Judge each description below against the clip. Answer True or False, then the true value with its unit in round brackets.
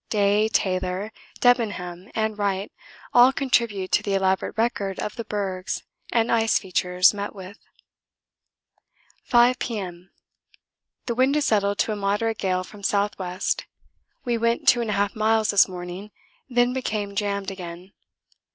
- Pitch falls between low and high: False (205 Hz)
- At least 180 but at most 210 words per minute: False (135 wpm)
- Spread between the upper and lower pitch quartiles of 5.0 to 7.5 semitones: False (3.1 semitones)